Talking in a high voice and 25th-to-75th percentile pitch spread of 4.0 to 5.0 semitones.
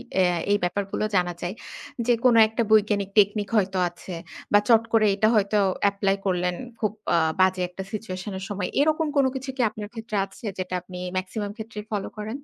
No: high, 205 Hz; average, 2.8 semitones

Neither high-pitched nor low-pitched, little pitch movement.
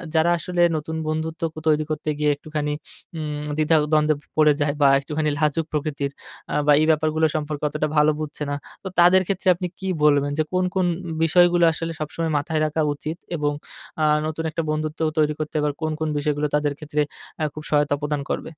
Yes: medium, 155 Hz; narrow, 1.3 semitones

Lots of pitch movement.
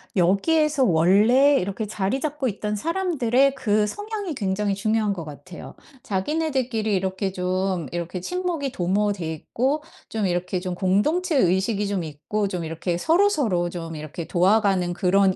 Yes: wide, 6.7 semitones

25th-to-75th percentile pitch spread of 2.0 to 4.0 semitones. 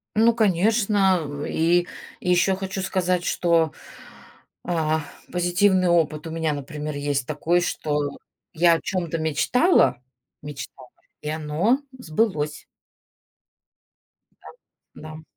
Yes: average, 3.6 semitones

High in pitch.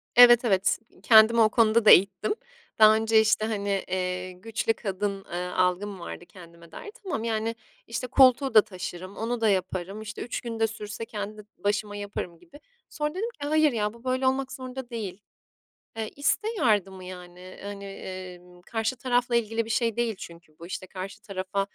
Yes: high, 215 Hz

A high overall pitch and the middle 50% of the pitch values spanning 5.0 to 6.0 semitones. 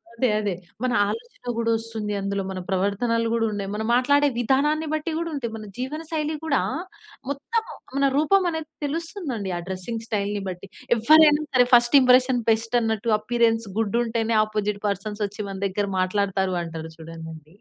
Yes: high, 230 Hz; wide, 5.5 semitones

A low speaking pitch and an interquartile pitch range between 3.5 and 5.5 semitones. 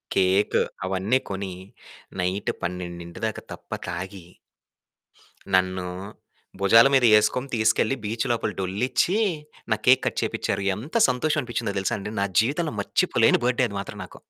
Yes: low, 105 Hz; average, 5.0 semitones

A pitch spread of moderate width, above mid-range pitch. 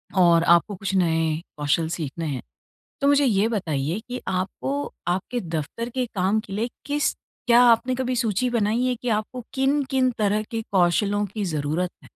No: wide, 6.2 semitones; high, 205 Hz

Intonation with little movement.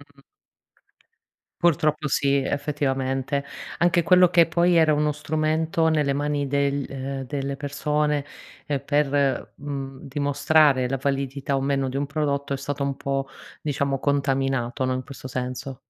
Yes: narrow, 1.7 semitones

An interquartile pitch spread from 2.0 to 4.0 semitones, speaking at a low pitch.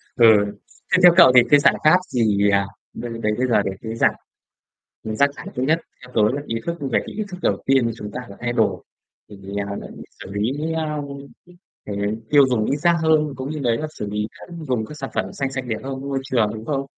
No: average, 4.8 semitones; low, 130 Hz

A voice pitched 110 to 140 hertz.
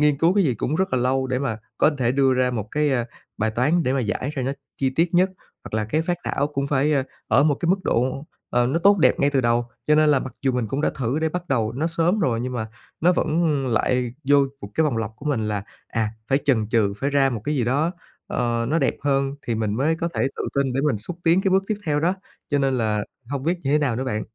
Yes: low, 135 Hz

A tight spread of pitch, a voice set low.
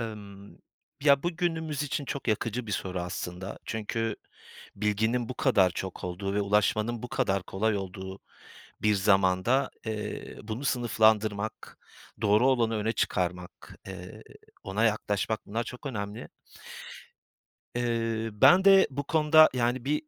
No: average, 3.7 semitones; low, 110 Hz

